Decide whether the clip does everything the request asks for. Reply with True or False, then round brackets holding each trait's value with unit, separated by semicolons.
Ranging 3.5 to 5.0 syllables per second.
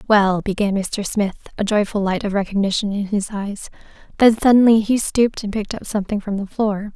False (5.5 syllables/s)